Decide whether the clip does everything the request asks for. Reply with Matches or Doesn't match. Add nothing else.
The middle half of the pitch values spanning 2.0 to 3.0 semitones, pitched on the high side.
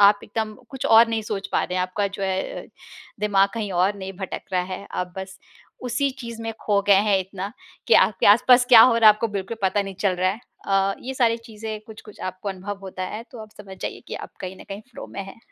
Matches